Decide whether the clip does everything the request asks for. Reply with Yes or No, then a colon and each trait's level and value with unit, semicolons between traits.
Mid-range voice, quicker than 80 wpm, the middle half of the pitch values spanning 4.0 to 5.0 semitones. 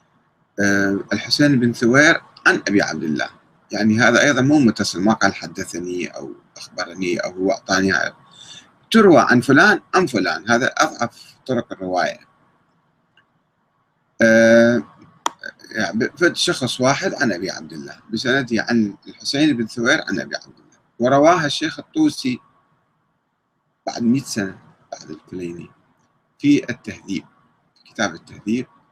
No: low, 115 Hz; average, 125 wpm; average, 4.3 semitones